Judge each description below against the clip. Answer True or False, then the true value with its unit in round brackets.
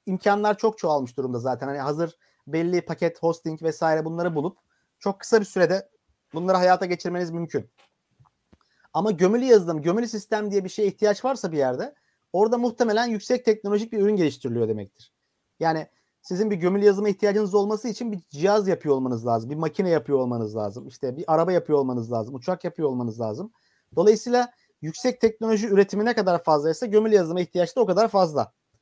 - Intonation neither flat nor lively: False (5.7 semitones)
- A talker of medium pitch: True (180 Hz)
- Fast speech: True (175 wpm)